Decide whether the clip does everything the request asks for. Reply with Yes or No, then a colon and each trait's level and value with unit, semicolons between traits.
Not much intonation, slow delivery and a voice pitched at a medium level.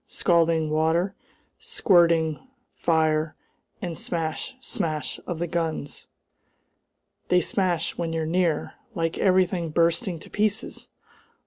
Yes: narrow, 1.8 semitones; slow, 110 wpm; medium, 165 Hz